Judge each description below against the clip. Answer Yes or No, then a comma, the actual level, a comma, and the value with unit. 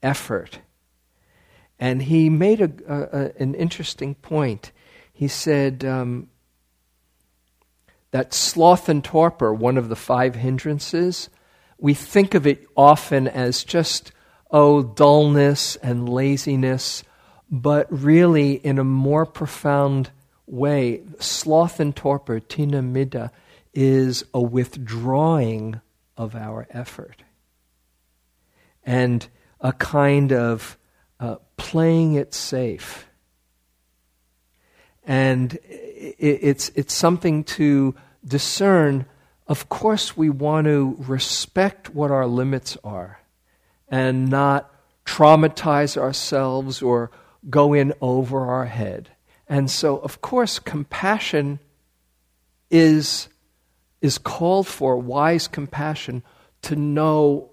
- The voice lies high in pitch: No, low, 135 Hz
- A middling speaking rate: No, slow, 100 wpm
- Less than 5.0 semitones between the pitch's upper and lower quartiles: Yes, average, 3.6 semitones